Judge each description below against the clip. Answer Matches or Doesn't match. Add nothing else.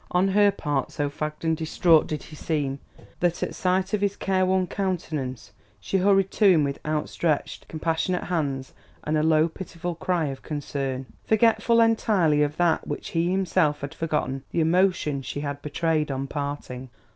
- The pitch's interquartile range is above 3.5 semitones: Matches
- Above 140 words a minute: Matches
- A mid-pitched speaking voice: Matches